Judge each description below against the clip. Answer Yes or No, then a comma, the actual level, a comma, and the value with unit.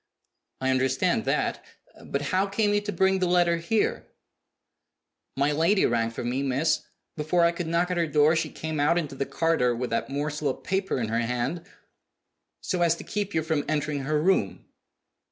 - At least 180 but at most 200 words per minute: Yes, average, 190 wpm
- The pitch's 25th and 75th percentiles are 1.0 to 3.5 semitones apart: No, average, 4.5 semitones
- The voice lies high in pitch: No, medium, 155 Hz